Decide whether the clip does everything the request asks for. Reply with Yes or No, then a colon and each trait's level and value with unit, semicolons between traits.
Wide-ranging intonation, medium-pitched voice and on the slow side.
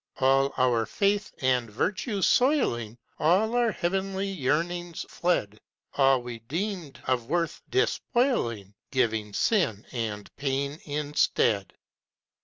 Yes: wide, 8.4 semitones; medium, 145 Hz; slow, 105 wpm